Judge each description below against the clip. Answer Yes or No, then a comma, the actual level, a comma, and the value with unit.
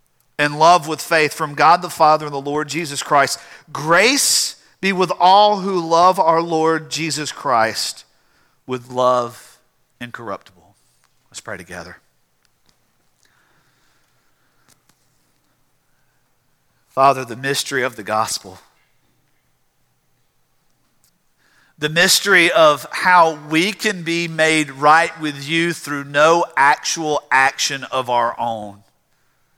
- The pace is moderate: No, slow, 110 wpm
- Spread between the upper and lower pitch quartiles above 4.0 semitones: Yes, average, 4.6 semitones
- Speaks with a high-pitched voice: No, medium, 145 Hz